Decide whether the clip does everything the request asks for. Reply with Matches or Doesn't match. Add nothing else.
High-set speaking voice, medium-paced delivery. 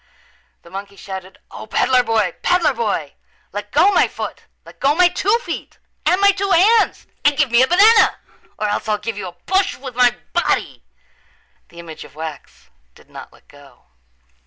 Matches